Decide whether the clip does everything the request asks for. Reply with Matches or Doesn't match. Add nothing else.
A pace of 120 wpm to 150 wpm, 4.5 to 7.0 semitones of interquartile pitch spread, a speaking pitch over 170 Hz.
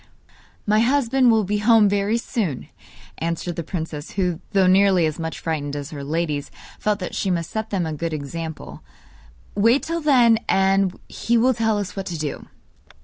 Doesn't match